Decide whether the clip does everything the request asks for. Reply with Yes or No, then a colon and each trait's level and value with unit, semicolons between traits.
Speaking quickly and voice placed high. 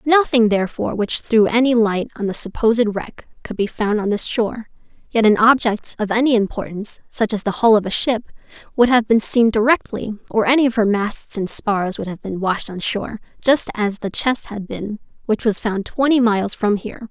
Yes: fast, 210 wpm; high, 220 Hz